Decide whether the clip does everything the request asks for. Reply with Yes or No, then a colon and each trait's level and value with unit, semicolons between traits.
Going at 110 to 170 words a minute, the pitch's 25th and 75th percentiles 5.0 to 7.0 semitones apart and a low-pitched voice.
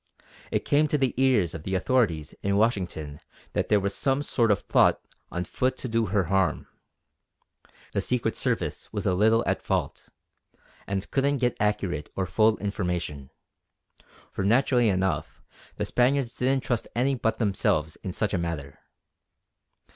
Yes: average, 160 wpm; wide, 5.5 semitones; low, 105 Hz